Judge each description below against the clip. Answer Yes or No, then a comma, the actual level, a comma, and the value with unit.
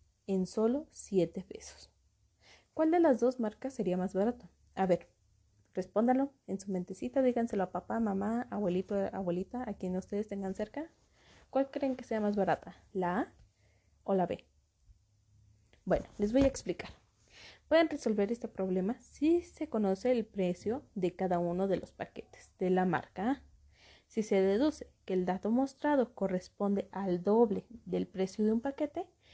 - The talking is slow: No, average, 160 wpm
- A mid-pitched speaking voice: No, high, 200 Hz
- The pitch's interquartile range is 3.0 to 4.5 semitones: No, average, 5.1 semitones